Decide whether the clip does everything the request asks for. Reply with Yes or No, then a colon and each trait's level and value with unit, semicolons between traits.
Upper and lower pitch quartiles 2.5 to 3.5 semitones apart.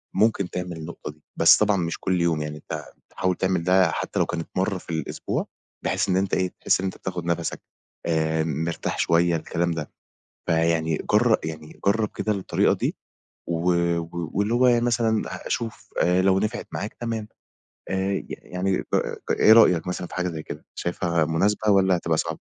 Yes: average, 3.2 semitones